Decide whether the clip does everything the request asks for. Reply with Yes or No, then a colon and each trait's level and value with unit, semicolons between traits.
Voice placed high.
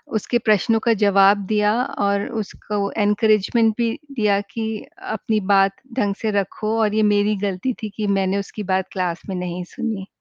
Yes: high, 205 Hz